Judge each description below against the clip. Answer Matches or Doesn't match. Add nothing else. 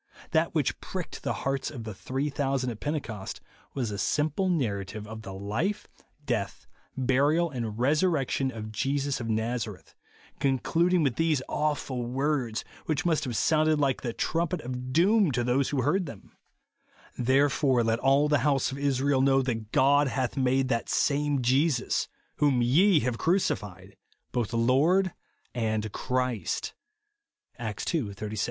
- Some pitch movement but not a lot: Matches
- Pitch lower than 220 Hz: Matches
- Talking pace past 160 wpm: Doesn't match